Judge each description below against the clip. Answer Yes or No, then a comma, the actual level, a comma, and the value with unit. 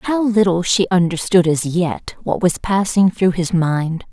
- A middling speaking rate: Yes, average, 175 wpm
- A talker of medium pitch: Yes, medium, 180 Hz